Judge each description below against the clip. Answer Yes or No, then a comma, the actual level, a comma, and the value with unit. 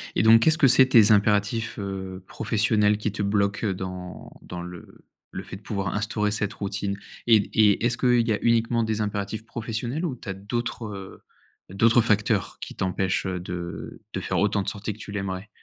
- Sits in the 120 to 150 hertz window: No, low, 105 Hz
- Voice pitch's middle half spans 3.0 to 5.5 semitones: No, narrow, 2.6 semitones